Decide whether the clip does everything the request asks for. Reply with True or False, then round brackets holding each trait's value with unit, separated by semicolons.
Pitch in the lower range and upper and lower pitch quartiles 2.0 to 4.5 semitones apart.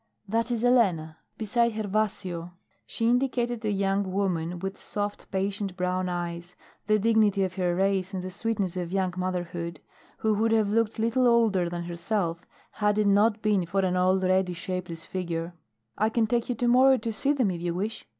False (195 Hz; 3.6 semitones)